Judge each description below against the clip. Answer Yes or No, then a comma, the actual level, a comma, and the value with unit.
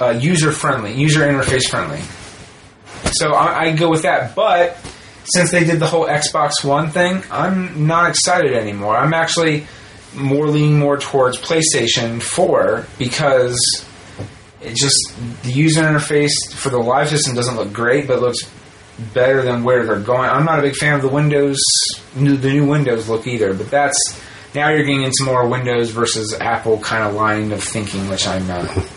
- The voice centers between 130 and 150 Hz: Yes, low, 135 Hz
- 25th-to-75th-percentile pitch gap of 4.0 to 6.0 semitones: Yes, average, 4.4 semitones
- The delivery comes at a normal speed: Yes, average, 170 wpm